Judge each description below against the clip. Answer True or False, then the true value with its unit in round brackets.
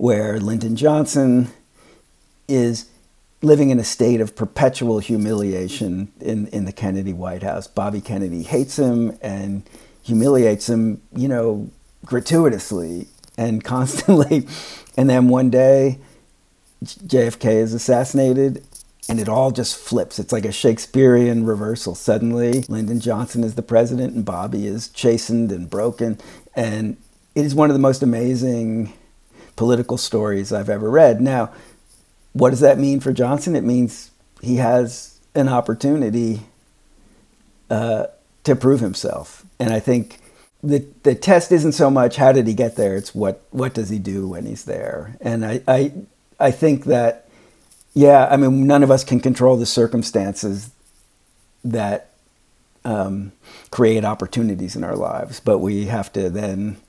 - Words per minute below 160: True (145 wpm)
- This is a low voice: True (120 Hz)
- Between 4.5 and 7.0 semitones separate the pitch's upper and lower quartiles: False (3.6 semitones)